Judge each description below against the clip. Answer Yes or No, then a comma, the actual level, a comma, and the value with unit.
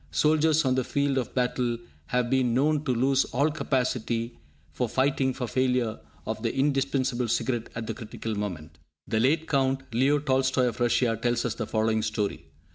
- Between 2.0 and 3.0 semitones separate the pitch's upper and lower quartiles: Yes, average, 2.7 semitones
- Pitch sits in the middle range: No, low, 125 Hz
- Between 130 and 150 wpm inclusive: No, average, 175 wpm